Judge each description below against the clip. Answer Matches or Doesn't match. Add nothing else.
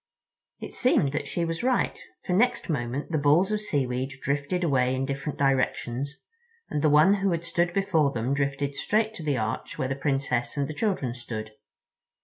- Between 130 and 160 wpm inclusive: Doesn't match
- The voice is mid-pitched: Matches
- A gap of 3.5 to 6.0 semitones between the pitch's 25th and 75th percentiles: Matches